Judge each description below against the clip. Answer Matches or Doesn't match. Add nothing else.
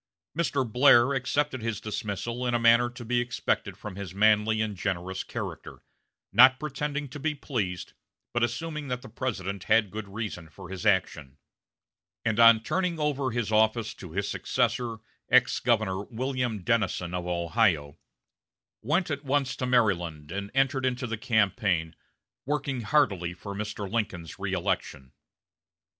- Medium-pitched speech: Doesn't match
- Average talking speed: Matches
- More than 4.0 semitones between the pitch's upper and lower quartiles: Matches